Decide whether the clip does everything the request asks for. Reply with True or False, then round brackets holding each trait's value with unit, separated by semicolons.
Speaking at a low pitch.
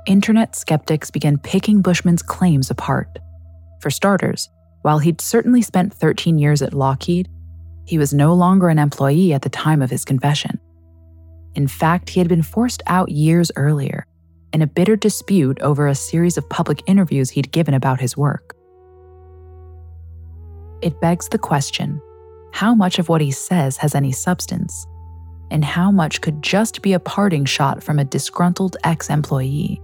False (150 Hz)